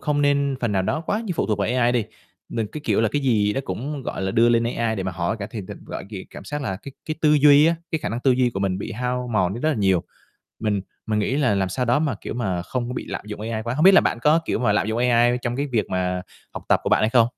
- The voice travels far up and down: No, average, 4.7 semitones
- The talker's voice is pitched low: Yes, low, 120 Hz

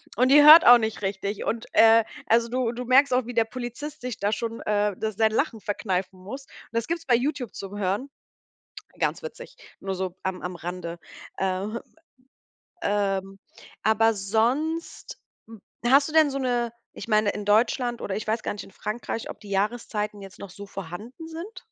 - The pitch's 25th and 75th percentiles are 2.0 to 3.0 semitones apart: No, average, 3.9 semitones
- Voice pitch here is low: No, high, 220 Hz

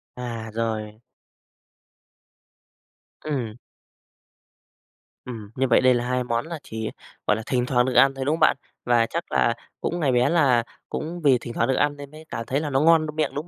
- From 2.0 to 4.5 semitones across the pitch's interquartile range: Yes, average, 3.9 semitones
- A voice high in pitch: No, low, 125 Hz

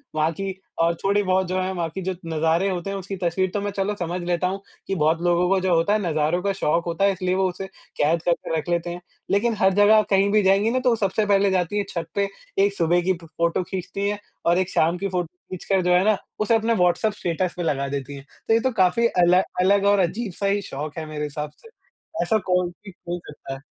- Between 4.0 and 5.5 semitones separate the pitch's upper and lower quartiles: No, average, 2.8 semitones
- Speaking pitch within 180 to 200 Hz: Yes, medium, 185 Hz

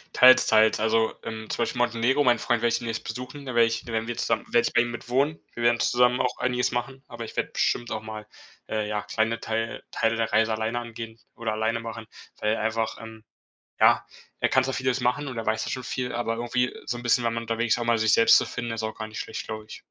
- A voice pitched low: Yes, low, 115 Hz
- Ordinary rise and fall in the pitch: No, narrow, 1.7 semitones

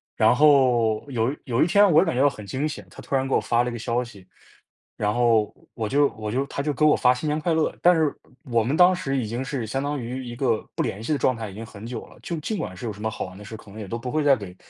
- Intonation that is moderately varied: Yes, average, 4.5 semitones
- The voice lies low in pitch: Yes, low, 125 Hz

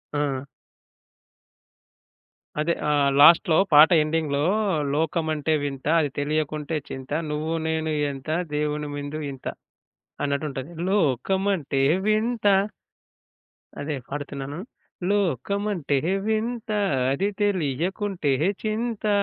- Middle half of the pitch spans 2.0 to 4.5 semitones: No, wide, 5.4 semitones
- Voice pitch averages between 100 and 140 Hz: No, medium, 155 Hz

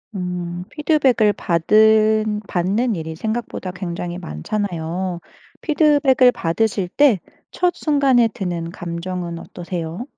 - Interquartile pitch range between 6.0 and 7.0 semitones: No, wide, 5.5 semitones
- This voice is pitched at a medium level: No, high, 195 Hz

